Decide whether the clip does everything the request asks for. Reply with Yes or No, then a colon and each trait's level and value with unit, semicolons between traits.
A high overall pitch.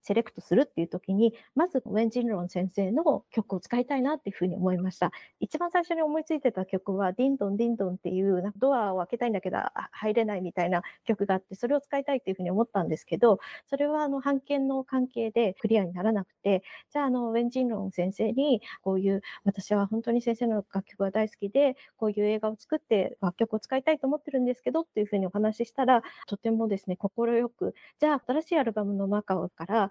Yes: high, 220 Hz